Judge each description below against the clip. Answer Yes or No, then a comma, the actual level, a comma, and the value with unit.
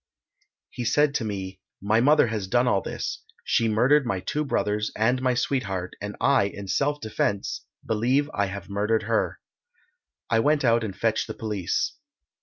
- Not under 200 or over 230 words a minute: No, average, 170 wpm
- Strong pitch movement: No, average, 4.1 semitones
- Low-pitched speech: Yes, low, 110 Hz